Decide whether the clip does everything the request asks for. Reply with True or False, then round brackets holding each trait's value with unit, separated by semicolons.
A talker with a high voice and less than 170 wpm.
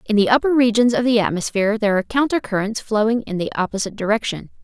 False (220 Hz; 205 wpm)